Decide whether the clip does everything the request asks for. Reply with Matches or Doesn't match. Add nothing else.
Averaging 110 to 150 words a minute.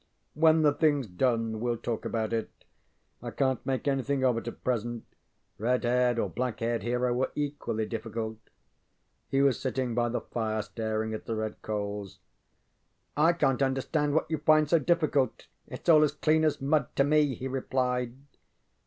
Doesn't match